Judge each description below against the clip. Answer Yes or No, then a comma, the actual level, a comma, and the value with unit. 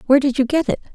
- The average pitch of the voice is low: No, very high, 270 Hz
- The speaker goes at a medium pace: No, fast, 320 wpm